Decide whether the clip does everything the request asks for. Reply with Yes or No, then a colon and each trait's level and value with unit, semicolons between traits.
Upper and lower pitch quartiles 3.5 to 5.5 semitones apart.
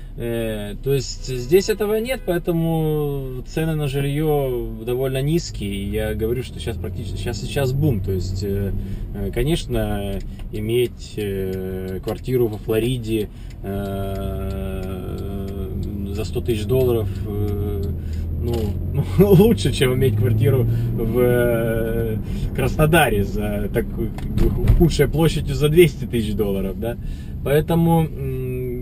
Yes: average, 5.2 semitones